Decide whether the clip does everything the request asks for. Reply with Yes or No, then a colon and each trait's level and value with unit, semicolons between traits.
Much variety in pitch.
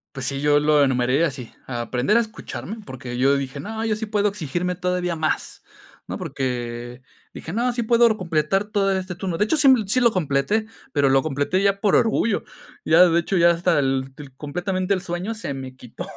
Yes: wide, 6.6 semitones